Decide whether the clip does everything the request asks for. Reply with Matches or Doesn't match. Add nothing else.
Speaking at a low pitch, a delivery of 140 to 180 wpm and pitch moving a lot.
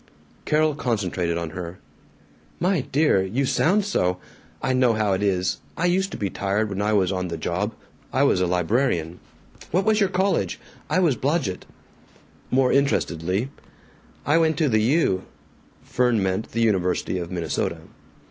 Matches